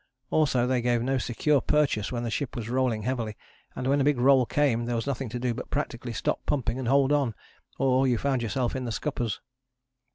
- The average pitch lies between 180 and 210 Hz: No, low, 125 Hz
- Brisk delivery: Yes, fast, 220 wpm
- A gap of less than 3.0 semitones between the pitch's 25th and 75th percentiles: Yes, narrow, 2.4 semitones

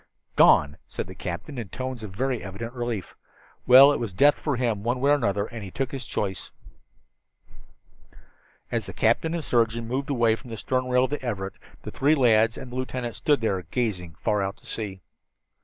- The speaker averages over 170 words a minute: Yes, fast, 205 wpm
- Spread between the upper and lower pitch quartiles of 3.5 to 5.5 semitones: Yes, average, 4.2 semitones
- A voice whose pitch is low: Yes, low, 115 Hz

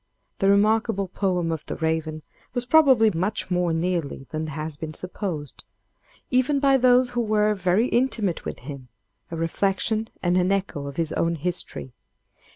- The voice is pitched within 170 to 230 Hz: Yes, medium, 185 Hz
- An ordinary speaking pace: Yes, average, 160 wpm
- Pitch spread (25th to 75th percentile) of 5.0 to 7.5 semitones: Yes, wide, 5.4 semitones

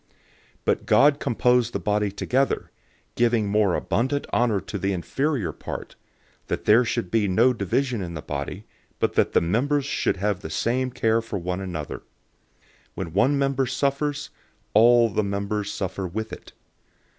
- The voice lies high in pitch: No, low, 110 Hz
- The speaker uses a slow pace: No, average, 165 wpm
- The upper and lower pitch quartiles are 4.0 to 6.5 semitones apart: Yes, average, 4.6 semitones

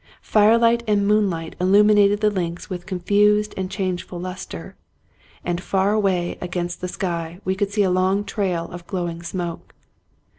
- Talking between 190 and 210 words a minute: No, average, 155 wpm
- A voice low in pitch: No, high, 190 Hz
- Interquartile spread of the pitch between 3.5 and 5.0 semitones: No, average, 2.7 semitones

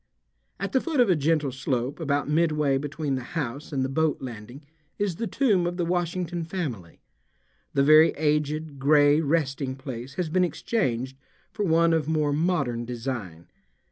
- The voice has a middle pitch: Yes, medium, 150 Hz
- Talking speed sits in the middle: Yes, average, 165 wpm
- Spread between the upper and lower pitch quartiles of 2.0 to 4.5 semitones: Yes, average, 3.9 semitones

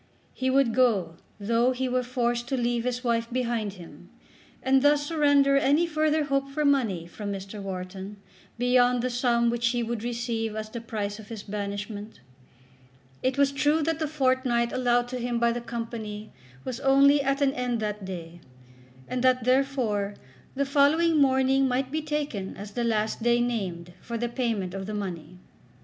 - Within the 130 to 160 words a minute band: No, average, 175 wpm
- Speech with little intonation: No, average, 4.1 semitones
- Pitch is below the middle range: No, high, 240 Hz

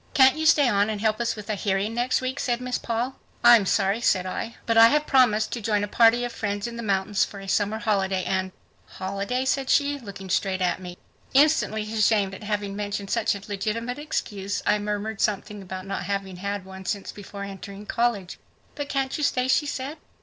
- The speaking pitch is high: Yes, high, 210 Hz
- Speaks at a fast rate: Yes, fast, 215 wpm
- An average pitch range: Yes, average, 3.4 semitones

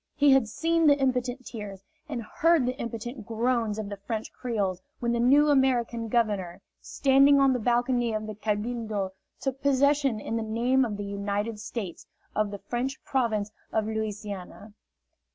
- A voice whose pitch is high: Yes, high, 230 Hz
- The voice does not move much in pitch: No, average, 3.8 semitones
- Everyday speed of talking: Yes, average, 165 wpm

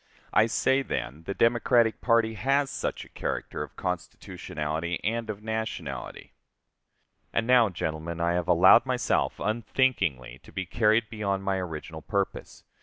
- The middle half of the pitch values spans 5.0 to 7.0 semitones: Yes, wide, 5.4 semitones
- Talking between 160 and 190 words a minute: No, average, 140 wpm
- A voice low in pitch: Yes, low, 105 Hz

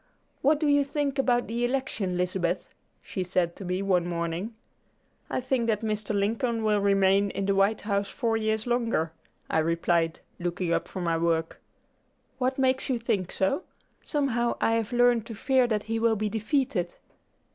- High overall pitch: Yes, high, 215 Hz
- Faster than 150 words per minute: Yes, average, 175 wpm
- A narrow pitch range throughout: No, average, 4.7 semitones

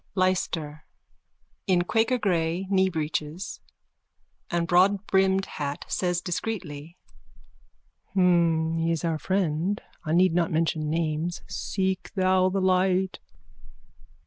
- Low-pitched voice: No, medium, 175 Hz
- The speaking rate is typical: No, slow, 95 wpm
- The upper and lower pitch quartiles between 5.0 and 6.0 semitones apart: No, average, 2.7 semitones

